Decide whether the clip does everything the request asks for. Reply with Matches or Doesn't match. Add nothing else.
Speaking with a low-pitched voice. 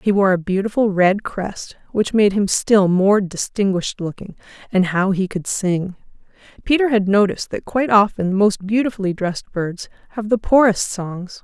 Doesn't match